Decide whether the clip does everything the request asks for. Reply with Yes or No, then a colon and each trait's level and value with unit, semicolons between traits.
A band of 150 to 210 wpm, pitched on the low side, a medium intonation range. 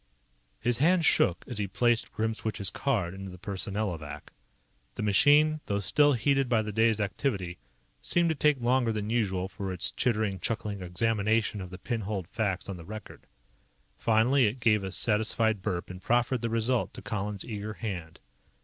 Yes: average, 170 wpm; low, 110 Hz; average, 3.5 semitones